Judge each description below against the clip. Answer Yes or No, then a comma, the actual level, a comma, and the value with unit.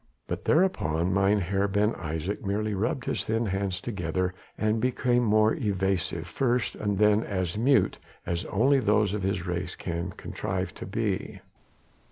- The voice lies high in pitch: No, low, 100 Hz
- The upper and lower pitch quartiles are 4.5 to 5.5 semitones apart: No, average, 3.0 semitones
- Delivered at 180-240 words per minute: No, average, 150 wpm